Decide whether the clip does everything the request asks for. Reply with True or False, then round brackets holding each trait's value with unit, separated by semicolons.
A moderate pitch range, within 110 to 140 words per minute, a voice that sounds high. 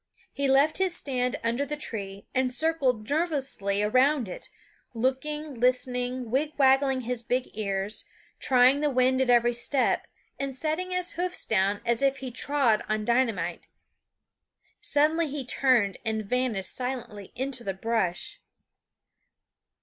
True (3.7 semitones; 135 wpm; 255 Hz)